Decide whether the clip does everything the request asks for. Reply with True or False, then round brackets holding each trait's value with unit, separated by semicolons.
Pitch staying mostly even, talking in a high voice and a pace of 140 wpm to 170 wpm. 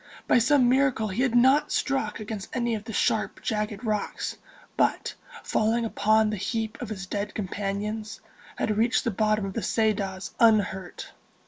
True (2.2 semitones; 215 Hz; 160 wpm)